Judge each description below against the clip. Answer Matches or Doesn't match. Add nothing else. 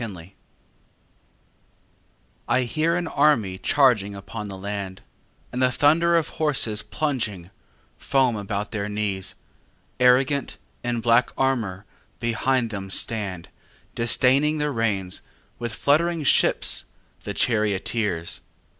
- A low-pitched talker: Matches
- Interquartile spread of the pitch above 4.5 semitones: Matches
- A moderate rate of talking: Doesn't match